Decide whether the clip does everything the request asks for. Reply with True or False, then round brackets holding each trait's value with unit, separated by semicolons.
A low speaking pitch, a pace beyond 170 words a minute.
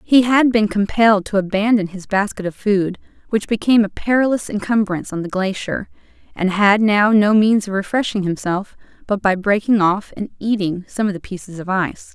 False (205 Hz; 190 wpm)